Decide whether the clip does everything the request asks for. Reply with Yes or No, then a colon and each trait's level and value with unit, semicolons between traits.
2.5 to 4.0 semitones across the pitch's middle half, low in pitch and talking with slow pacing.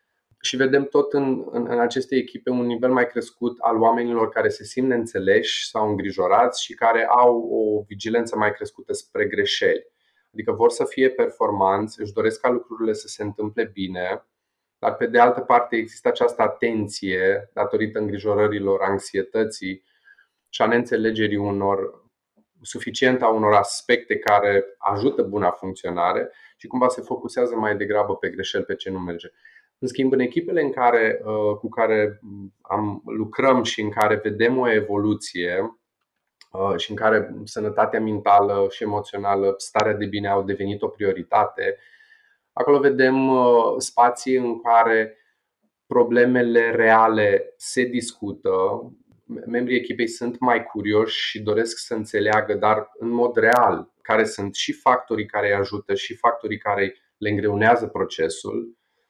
No: average, 3.6 semitones; low, 115 Hz; average, 145 wpm